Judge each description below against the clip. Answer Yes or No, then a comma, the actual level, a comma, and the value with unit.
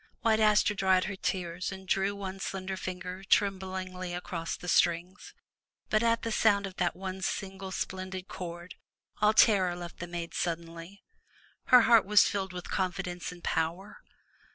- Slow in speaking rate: No, average, 165 wpm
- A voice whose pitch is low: No, medium, 185 Hz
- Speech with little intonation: Yes, narrow, 2.0 semitones